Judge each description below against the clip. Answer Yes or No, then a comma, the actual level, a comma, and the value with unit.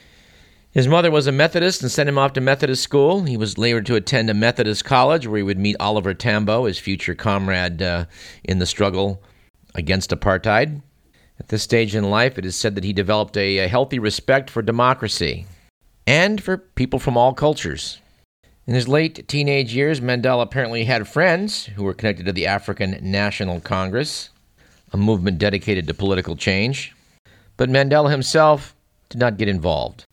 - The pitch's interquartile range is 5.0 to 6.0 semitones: Yes, average, 5.3 semitones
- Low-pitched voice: Yes, low, 105 Hz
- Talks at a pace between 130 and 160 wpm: No, average, 175 wpm